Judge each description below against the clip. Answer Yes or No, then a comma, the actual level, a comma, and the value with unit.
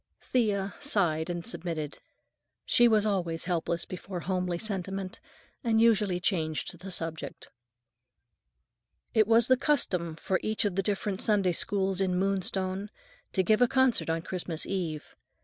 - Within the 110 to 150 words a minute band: Yes, average, 140 wpm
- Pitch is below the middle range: No, high, 190 Hz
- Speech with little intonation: No, average, 3.5 semitones